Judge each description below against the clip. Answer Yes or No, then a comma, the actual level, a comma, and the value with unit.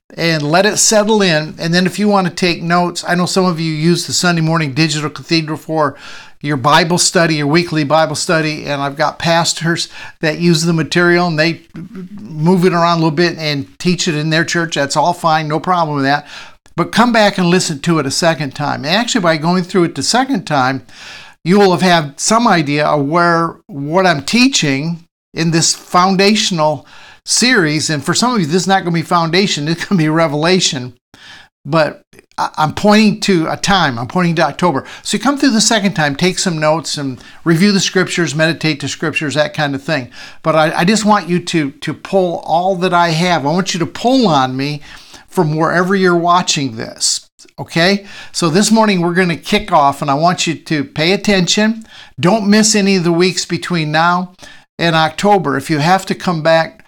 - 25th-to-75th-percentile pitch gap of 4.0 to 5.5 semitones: No, average, 3.2 semitones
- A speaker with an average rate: No, fast, 210 wpm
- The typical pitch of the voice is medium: Yes, medium, 170 Hz